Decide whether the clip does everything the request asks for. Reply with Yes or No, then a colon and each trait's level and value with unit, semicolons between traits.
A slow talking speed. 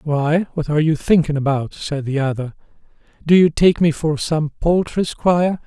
No: average, 180 wpm